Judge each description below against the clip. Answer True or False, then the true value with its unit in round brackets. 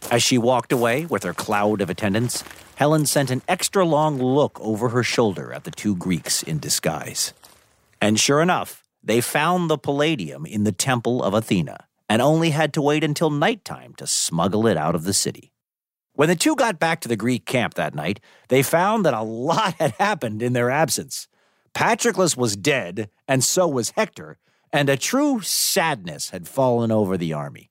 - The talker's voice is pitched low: True (130 Hz)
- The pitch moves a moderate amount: False (6.5 semitones)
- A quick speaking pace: False (190 wpm)